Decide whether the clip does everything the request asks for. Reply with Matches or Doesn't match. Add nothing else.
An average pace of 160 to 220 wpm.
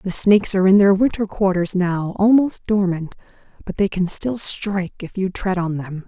Matches